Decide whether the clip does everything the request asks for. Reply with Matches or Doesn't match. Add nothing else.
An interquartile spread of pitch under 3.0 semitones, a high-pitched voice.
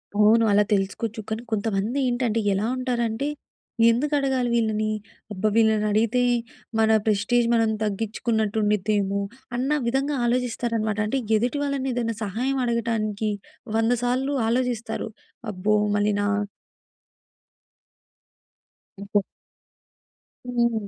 Matches